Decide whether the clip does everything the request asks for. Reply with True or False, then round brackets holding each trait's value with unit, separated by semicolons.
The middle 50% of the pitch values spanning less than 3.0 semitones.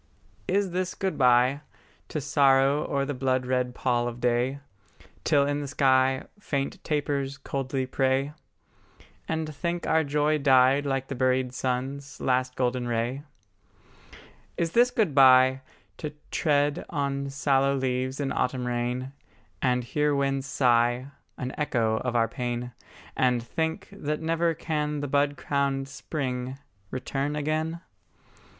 True (2.4 semitones)